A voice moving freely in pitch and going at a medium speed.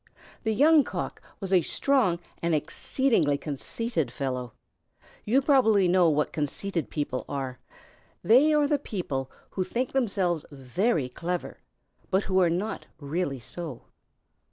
No: wide, 7.7 semitones; slow, 130 wpm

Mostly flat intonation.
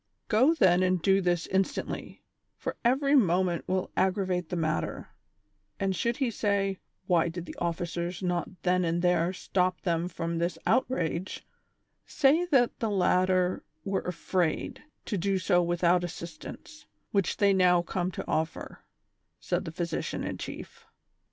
Yes: narrow, 2.3 semitones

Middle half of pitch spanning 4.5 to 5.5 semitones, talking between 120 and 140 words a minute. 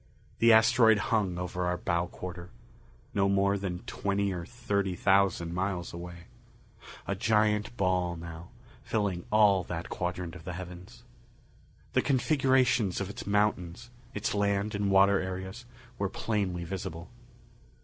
No: average, 2.8 semitones; slow, 135 wpm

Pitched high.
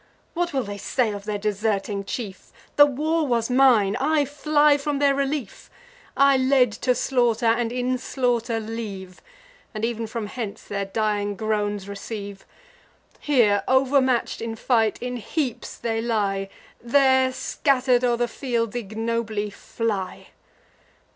Yes: high, 235 Hz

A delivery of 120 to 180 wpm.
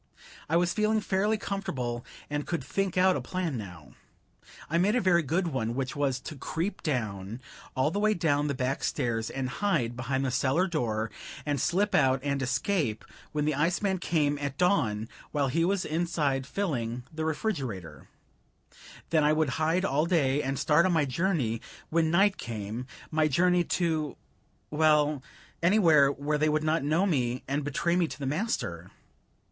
Yes: average, 175 wpm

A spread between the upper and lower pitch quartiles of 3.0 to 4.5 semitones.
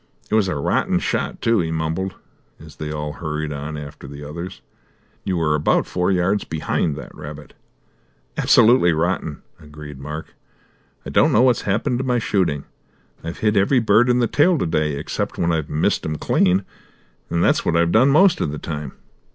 No: wide, 5.4 semitones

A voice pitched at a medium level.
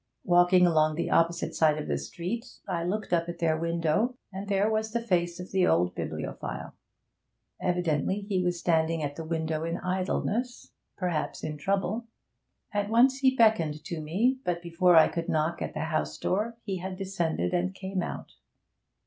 Yes: medium, 175 Hz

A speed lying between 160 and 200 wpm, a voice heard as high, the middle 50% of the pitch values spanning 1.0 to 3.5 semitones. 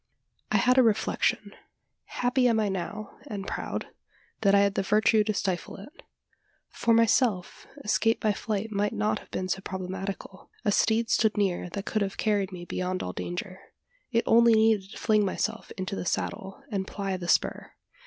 Yes: average, 180 wpm; high, 205 Hz; narrow, 2.6 semitones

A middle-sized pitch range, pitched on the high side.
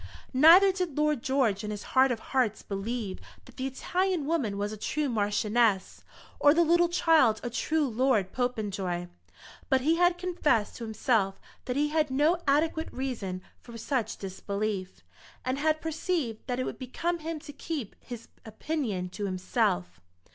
No: wide, 6.7 semitones; very high, 255 Hz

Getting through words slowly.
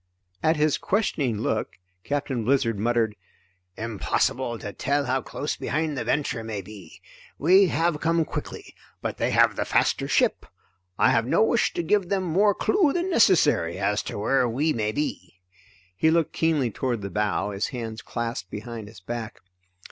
No: average, 170 wpm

